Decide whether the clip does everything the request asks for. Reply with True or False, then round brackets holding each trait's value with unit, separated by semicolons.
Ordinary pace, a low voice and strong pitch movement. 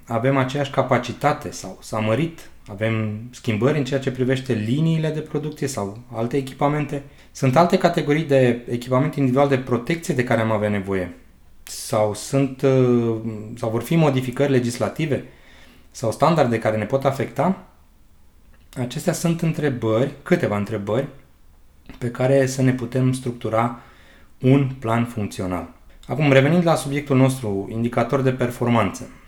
False (135 wpm; 125 Hz; 4.2 semitones)